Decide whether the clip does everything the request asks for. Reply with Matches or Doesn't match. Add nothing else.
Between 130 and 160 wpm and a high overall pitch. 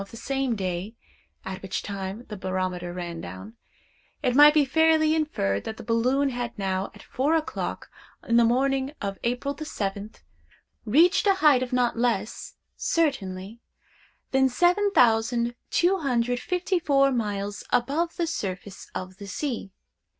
Matches